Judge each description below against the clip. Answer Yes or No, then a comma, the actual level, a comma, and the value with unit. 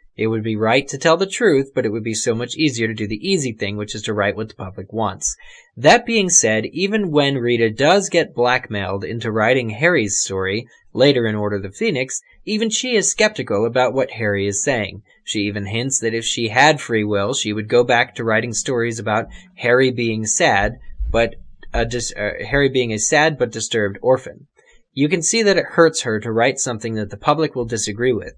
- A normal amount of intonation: Yes, average, 4.9 semitones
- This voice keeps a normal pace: No, fast, 220 wpm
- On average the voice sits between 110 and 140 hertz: Yes, low, 115 Hz